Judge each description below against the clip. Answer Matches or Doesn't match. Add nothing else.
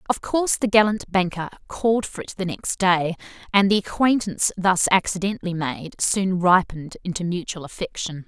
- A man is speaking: Doesn't match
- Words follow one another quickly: Doesn't match